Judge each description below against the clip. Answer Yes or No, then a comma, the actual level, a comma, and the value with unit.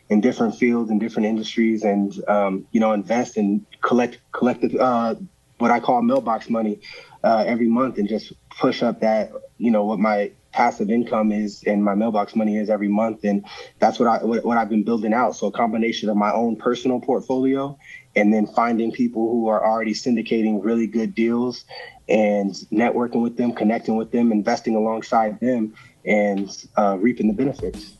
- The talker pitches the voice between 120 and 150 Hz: No, low, 110 Hz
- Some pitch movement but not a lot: No, narrow, 1.9 semitones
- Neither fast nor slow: Yes, average, 185 wpm